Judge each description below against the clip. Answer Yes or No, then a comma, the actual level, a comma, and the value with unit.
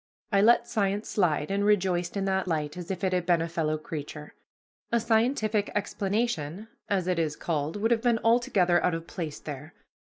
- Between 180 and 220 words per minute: Yes, average, 190 wpm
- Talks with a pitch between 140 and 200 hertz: Yes, medium, 185 Hz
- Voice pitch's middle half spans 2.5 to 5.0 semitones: Yes, average, 4.3 semitones